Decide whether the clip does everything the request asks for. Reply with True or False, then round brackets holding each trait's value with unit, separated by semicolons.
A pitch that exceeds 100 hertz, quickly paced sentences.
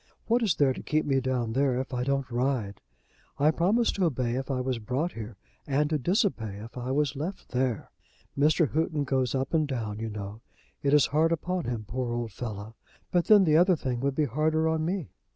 True (135 Hz; 215 wpm)